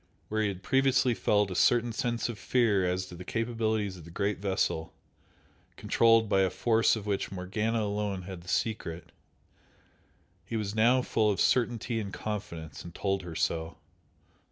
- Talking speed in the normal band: Yes, average, 170 wpm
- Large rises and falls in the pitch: No, average, 3.5 semitones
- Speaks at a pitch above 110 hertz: No, low, 105 Hz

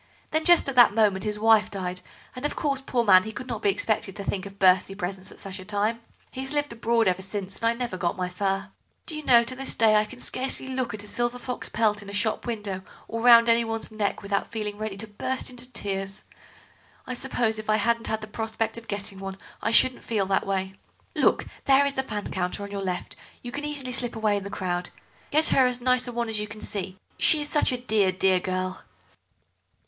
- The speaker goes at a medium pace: No, fast, 235 wpm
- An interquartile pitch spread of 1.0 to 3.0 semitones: No, average, 3.8 semitones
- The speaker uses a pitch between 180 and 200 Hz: No, high, 215 Hz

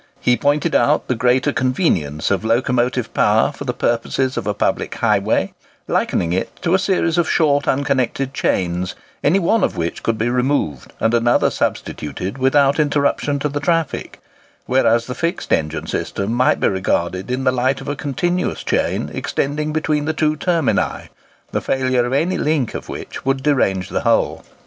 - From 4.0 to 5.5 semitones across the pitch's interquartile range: Yes, average, 4.3 semitones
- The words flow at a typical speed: Yes, average, 175 wpm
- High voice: No, low, 130 Hz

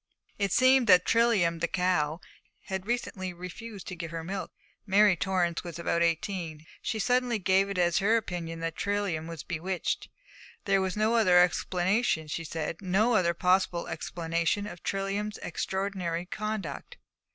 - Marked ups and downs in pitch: No, average, 3.2 semitones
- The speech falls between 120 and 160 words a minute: Yes, average, 150 wpm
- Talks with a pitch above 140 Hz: Yes, medium, 185 Hz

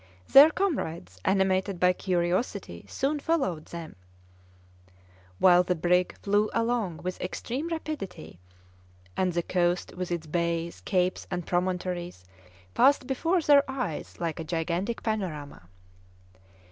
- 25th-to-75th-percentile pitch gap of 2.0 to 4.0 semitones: No, average, 5.3 semitones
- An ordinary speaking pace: No, slow, 120 wpm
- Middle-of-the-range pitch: Yes, medium, 180 Hz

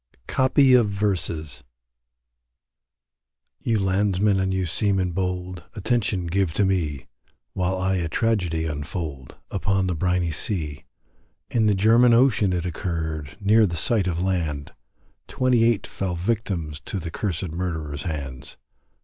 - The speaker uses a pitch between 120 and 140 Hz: No, very low, 95 Hz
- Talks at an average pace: No, slow, 130 wpm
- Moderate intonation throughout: Yes, average, 4.0 semitones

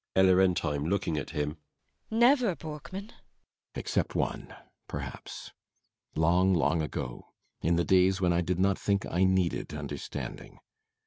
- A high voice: No, very low, 90 Hz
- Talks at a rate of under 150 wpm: Yes, slow, 135 wpm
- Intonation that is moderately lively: Yes, average, 3.0 semitones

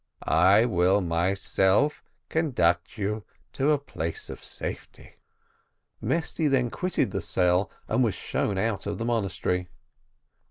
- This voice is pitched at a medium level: No, low, 100 Hz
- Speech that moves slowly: Yes, slow, 125 wpm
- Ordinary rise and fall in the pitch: No, wide, 6.2 semitones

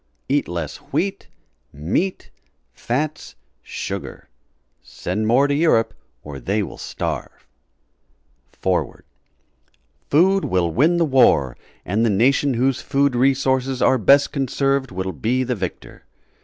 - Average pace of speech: No, slow, 120 wpm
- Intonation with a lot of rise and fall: Yes, wide, 6.4 semitones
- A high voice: No, low, 130 Hz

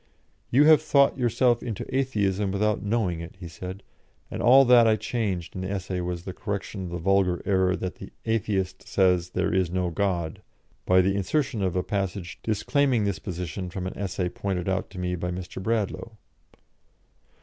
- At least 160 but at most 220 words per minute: Yes, average, 180 wpm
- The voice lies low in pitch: Yes, very low, 95 Hz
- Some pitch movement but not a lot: Yes, average, 3.3 semitones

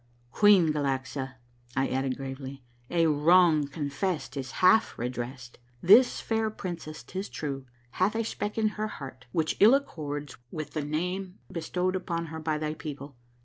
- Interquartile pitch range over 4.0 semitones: Yes, average, 5.2 semitones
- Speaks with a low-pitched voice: No, medium, 155 Hz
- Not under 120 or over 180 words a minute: Yes, average, 160 wpm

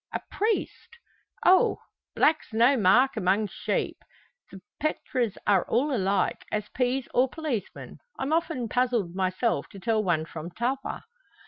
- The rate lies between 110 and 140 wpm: Yes, slow, 135 wpm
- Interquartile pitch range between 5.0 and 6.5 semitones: Yes, wide, 5.5 semitones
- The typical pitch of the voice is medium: No, high, 235 Hz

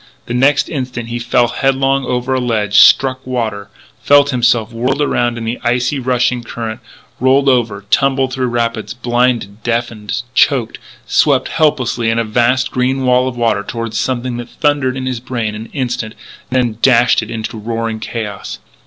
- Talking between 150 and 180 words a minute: Yes, average, 165 wpm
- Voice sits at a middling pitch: No, low, 120 Hz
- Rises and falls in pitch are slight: Yes, narrow, 2.0 semitones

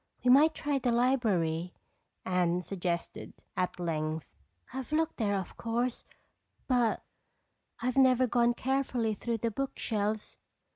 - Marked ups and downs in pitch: Yes, wide, 5.8 semitones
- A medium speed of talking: No, slow, 130 wpm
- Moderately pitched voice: No, high, 230 Hz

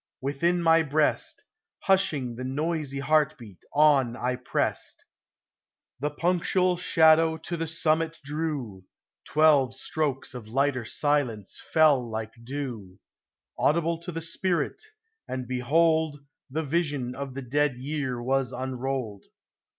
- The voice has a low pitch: No, medium, 145 Hz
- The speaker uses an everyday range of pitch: Yes, average, 4.0 semitones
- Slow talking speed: Yes, slow, 120 wpm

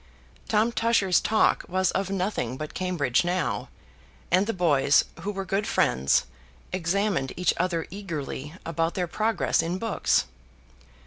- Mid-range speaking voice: Yes, medium, 180 Hz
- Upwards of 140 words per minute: No, slow, 135 wpm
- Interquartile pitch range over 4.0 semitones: No, average, 3.4 semitones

